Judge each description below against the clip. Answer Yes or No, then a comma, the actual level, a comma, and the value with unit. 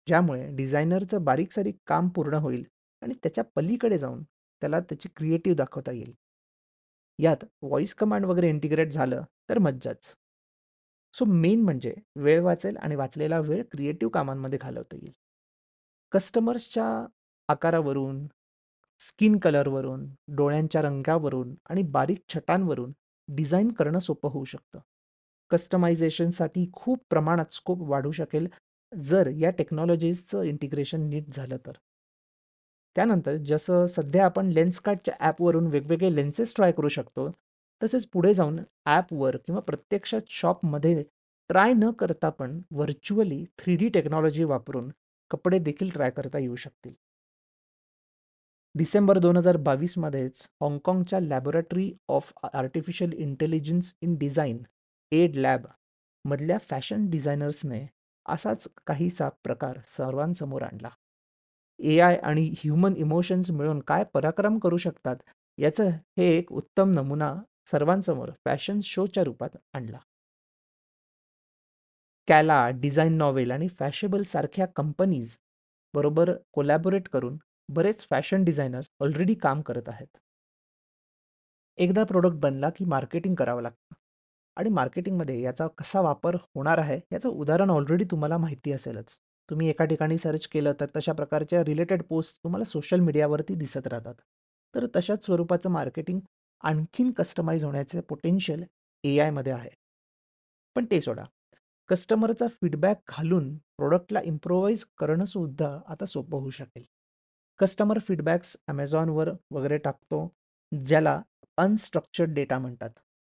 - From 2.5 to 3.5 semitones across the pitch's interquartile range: No, average, 4.1 semitones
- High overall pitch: No, medium, 160 Hz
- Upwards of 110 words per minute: Yes, average, 120 wpm